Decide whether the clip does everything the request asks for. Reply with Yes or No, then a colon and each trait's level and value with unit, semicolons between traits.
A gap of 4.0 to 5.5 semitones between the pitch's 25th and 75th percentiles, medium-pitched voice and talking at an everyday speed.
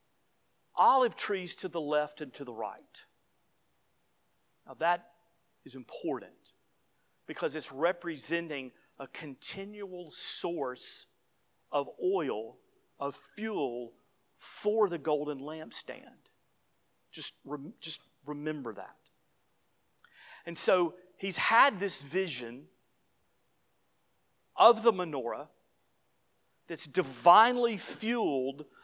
No: average, 4.8 semitones; medium, 170 Hz; slow, 90 wpm